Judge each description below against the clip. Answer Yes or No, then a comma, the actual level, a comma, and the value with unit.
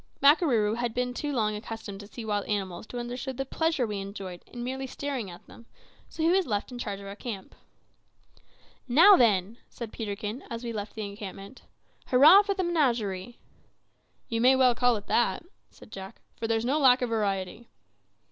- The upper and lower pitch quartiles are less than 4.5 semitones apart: Yes, average, 4.0 semitones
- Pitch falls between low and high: No, high, 230 Hz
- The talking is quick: No, average, 185 wpm